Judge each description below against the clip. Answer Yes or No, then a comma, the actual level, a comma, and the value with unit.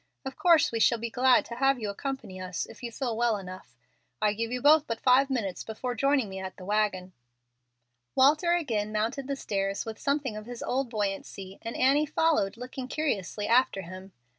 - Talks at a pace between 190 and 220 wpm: Yes, average, 195 wpm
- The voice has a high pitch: Yes, high, 230 Hz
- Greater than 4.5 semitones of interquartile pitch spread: Yes, average, 5.0 semitones